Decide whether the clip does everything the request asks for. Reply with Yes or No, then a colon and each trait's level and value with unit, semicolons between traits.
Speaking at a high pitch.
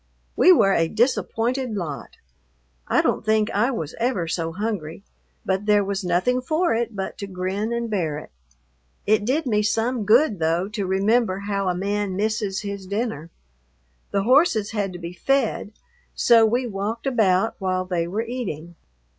Yes: high, 205 Hz